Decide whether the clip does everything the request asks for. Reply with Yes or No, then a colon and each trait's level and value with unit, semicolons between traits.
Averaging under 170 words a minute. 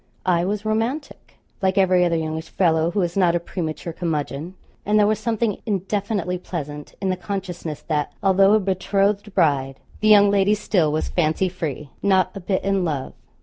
No: average, 180 wpm